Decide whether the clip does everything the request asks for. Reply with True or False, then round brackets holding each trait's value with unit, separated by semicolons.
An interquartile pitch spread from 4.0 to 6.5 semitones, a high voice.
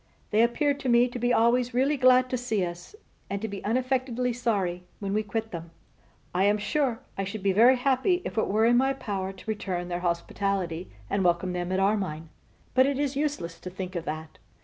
True (5.3 semitones; 215 Hz)